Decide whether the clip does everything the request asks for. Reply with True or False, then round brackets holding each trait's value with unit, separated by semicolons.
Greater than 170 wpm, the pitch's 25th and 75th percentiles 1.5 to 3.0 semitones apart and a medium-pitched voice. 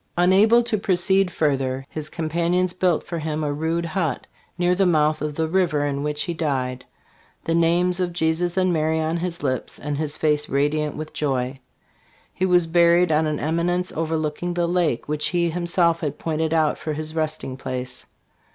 True (185 wpm; 2.7 semitones; 160 Hz)